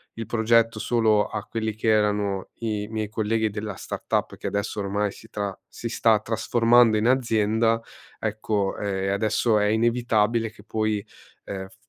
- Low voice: Yes, low, 110 Hz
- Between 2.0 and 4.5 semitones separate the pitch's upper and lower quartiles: No, narrow, 1.6 semitones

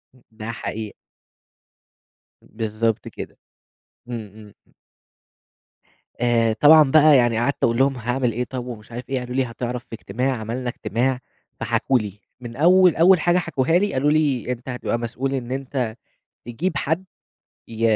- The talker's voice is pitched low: Yes, low, 125 Hz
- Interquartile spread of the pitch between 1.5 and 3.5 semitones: Yes, average, 2.9 semitones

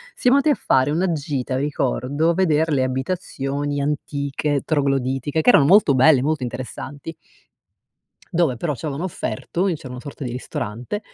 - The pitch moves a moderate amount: Yes, average, 3.5 semitones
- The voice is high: No, medium, 145 Hz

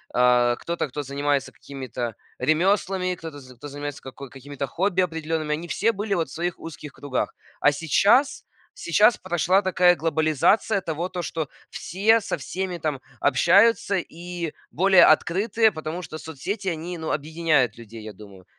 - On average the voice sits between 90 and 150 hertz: No, medium, 160 Hz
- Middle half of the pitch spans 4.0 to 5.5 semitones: Yes, average, 4.4 semitones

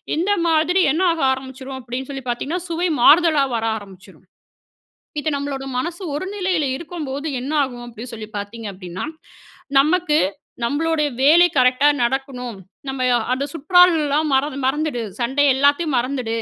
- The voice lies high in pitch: Yes, very high, 280 Hz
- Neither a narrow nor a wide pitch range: Yes, average, 4.0 semitones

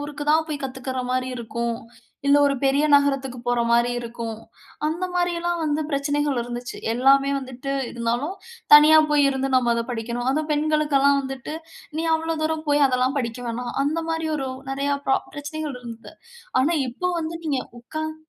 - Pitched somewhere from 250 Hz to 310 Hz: Yes, very high, 275 Hz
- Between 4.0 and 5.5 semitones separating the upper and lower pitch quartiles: No, average, 3.5 semitones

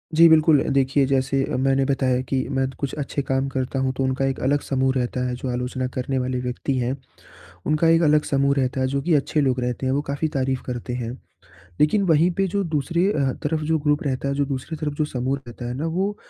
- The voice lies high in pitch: No, low, 135 Hz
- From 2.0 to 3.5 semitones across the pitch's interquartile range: Yes, narrow, 2.5 semitones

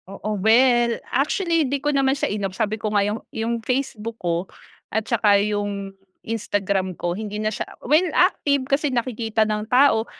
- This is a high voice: Yes, high, 220 Hz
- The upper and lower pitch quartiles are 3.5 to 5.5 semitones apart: Yes, average, 4.1 semitones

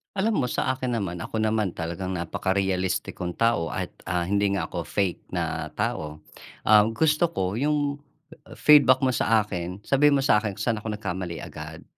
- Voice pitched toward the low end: Yes, low, 105 Hz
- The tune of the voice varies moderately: No, wide, 6.2 semitones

